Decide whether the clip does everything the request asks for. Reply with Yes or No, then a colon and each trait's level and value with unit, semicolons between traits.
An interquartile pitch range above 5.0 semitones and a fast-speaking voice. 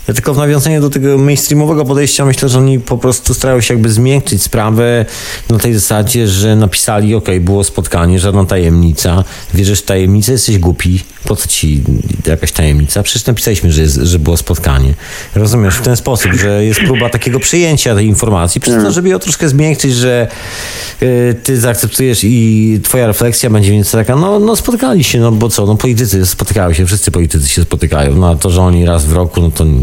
Yes: wide, 5.5 semitones; fast, 195 wpm